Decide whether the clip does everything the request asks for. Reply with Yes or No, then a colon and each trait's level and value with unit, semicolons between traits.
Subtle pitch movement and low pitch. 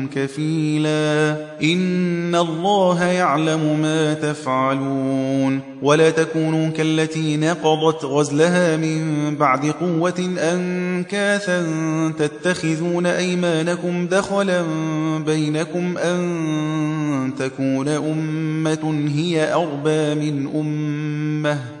No: narrow, 2.3 semitones; medium, 155 Hz